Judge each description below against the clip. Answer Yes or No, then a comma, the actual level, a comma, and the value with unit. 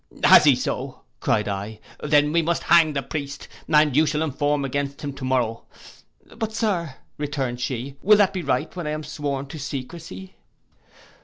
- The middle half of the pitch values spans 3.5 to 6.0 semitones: No, average, 3.1 semitones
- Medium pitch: Yes, medium, 145 Hz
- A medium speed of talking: Yes, average, 170 wpm